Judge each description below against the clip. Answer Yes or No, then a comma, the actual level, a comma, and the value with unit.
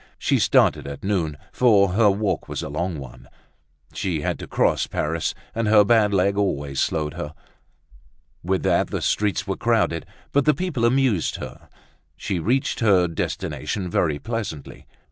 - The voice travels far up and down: Yes, wide, 6.0 semitones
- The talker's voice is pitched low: Yes, very low, 95 Hz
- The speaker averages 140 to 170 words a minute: Yes, average, 160 wpm